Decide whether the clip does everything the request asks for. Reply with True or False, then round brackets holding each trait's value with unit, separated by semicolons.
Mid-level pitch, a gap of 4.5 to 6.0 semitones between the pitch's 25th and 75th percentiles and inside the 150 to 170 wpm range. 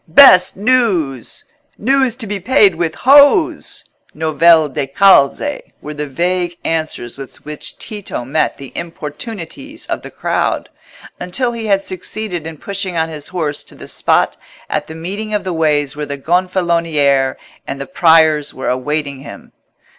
True (165 Hz; 5.2 semitones; 155 wpm)